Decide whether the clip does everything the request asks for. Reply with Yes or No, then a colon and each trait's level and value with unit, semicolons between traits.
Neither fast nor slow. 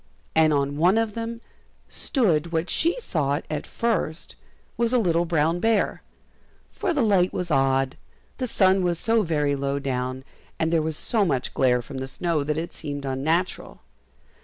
Yes: average, 170 wpm